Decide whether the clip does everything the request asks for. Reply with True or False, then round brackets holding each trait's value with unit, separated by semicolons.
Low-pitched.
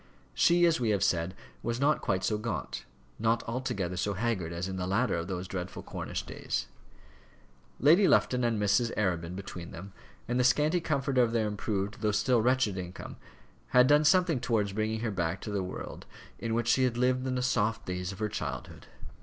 True (110 Hz)